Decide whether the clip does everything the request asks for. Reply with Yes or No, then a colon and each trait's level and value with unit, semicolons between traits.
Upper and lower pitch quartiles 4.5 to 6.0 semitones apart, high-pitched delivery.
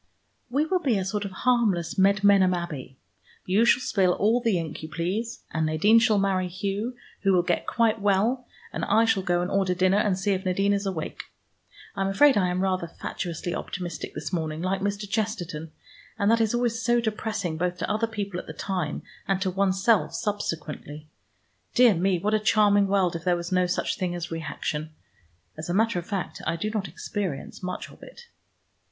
No: average, 3.3 semitones; high, 195 Hz